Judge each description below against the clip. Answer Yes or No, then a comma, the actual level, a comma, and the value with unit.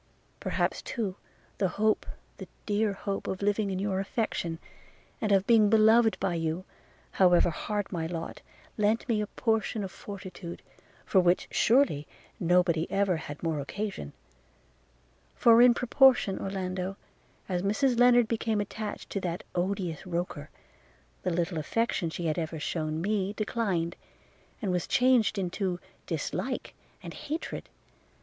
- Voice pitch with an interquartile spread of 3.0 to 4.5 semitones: Yes, average, 3.7 semitones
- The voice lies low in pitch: No, high, 195 Hz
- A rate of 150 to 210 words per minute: No, average, 140 wpm